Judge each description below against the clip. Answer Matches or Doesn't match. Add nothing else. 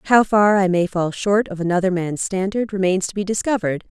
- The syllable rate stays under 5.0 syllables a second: Doesn't match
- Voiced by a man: Doesn't match